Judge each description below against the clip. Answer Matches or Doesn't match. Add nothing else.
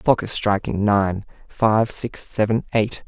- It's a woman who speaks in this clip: Doesn't match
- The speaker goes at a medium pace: Matches